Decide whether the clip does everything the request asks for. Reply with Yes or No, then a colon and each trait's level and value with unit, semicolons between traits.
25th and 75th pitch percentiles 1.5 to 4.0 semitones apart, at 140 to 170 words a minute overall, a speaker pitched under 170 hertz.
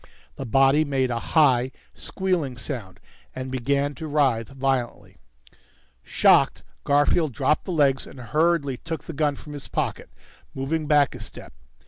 Yes: average, 2.7 semitones; average, 145 wpm; medium, 140 Hz